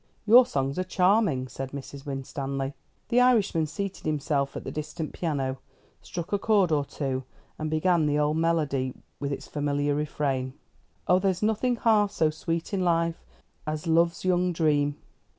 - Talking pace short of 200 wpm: Yes, average, 160 wpm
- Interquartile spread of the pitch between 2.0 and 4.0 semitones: No, average, 4.4 semitones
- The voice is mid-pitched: Yes, medium, 155 Hz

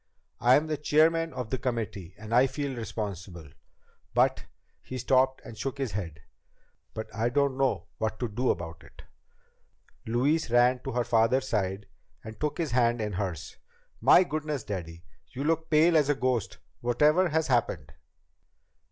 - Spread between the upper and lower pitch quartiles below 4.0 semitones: No, average, 5.1 semitones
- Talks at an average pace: Yes, average, 165 wpm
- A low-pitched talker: Yes, low, 120 Hz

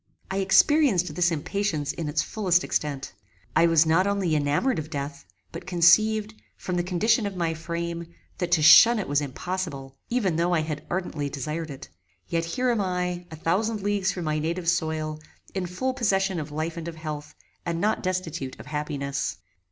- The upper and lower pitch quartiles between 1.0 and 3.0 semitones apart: No, average, 3.7 semitones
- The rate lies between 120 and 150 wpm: No, average, 185 wpm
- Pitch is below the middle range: No, medium, 170 Hz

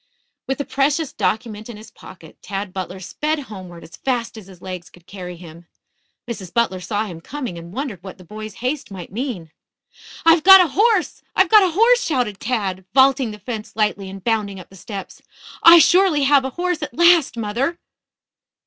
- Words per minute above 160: Yes, average, 190 wpm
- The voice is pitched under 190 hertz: No, high, 225 Hz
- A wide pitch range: Yes, wide, 7.4 semitones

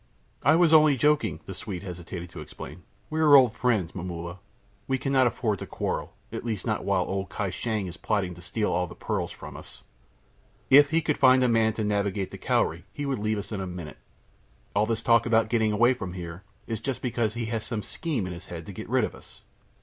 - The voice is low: Yes, low, 110 Hz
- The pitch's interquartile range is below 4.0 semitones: No, average, 5.3 semitones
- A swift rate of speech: Yes, fast, 225 wpm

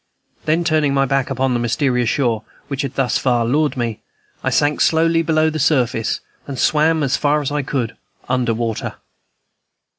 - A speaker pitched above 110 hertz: Yes, low, 135 Hz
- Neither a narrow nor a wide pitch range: Yes, average, 3.8 semitones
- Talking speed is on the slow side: No, average, 175 wpm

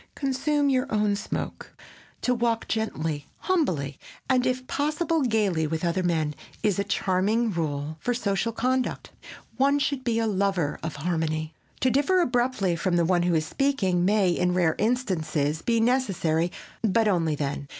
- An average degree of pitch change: No, wide, 7.2 semitones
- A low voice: No, high, 200 Hz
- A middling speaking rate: Yes, average, 160 wpm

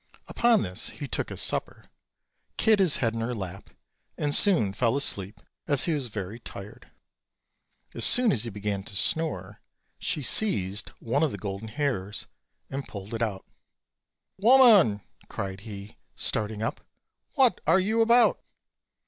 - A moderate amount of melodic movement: No, wide, 8.3 semitones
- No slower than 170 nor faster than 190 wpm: No, average, 150 wpm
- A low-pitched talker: Yes, low, 115 Hz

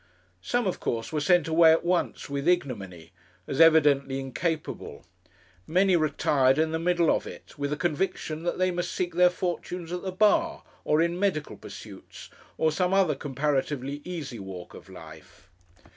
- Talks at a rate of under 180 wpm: Yes, average, 165 wpm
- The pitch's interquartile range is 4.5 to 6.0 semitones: No, average, 4.1 semitones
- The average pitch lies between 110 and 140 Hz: No, medium, 160 Hz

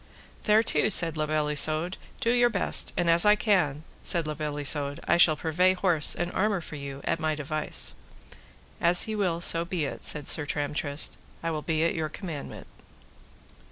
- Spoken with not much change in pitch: No, average, 3.1 semitones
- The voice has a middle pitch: Yes, medium, 160 Hz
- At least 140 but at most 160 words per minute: No, average, 185 wpm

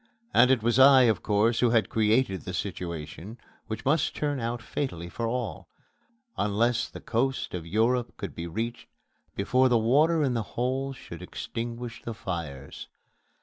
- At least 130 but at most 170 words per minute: Yes, average, 160 wpm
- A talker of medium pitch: No, low, 115 Hz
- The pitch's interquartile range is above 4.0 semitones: No, average, 3.7 semitones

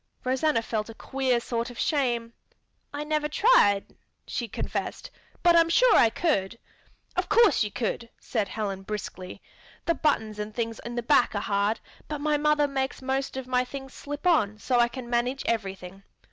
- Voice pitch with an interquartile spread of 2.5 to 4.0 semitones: No, average, 5.1 semitones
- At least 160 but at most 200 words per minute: Yes, average, 180 wpm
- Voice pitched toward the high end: Yes, high, 245 Hz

